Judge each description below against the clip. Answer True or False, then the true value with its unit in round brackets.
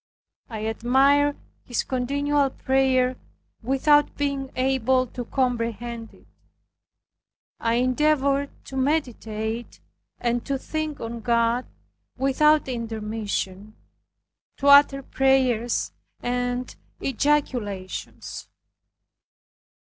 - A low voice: False (255 Hz)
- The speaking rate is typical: False (80 wpm)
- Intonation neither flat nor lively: True (3.0 semitones)